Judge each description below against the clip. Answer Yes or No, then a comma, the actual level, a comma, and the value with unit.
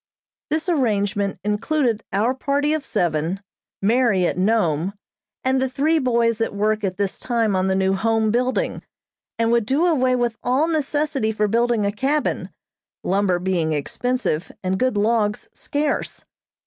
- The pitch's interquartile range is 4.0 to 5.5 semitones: Yes, average, 4.7 semitones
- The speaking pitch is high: Yes, high, 225 Hz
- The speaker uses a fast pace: No, average, 150 wpm